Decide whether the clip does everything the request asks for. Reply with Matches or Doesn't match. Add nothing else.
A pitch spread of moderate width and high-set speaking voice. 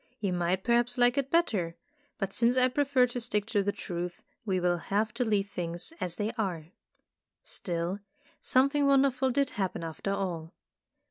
Doesn't match